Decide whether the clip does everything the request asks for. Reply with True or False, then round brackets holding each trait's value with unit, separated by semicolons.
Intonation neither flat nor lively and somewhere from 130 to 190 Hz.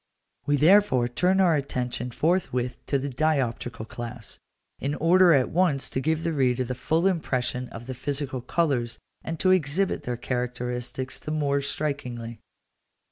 True (4.4 semitones; 135 Hz)